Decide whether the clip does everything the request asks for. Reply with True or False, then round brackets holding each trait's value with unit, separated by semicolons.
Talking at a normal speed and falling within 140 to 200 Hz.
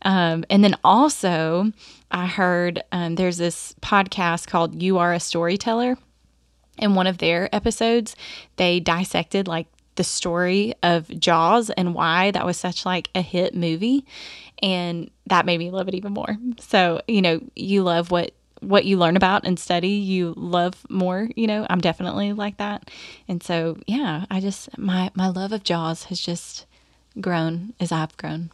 True (170 wpm; 185 Hz)